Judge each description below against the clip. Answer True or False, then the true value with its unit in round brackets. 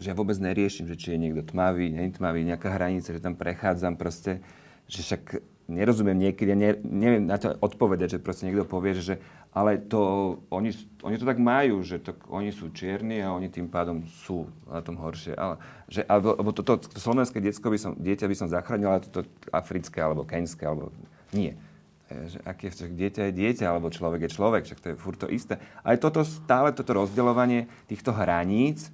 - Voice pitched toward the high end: False (95 Hz)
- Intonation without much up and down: False (3.3 semitones)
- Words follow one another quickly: True (205 wpm)